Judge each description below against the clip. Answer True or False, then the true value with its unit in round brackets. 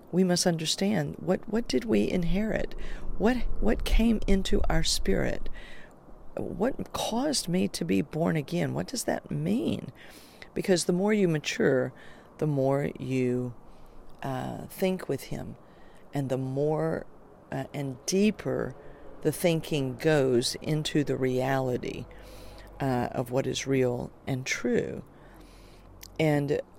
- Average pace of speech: False (130 wpm)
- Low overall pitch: False (155 Hz)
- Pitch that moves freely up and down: True (6.2 semitones)